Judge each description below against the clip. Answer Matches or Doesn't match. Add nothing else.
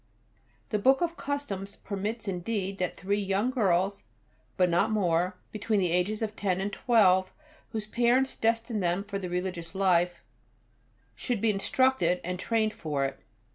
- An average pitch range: Matches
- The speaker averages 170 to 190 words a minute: Doesn't match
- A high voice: Matches